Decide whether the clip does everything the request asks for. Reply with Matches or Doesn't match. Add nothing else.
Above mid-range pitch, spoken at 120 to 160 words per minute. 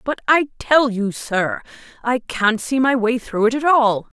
Doesn't match